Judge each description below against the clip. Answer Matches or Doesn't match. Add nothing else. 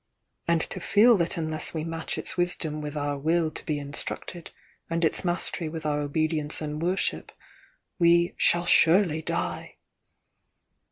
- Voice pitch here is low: Doesn't match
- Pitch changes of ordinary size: Doesn't match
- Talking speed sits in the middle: Matches